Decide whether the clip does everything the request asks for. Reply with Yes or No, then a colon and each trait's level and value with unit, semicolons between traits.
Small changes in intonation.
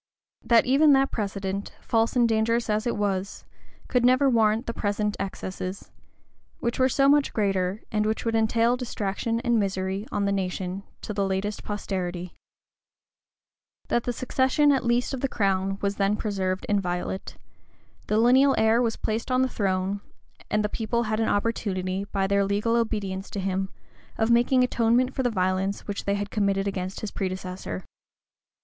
No: average, 3.3 semitones